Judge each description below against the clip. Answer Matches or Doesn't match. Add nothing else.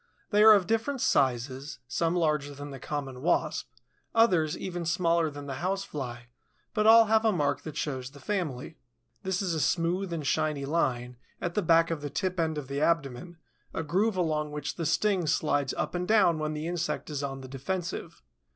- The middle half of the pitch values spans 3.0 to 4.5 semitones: Matches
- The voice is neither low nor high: Matches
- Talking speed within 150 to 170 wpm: Doesn't match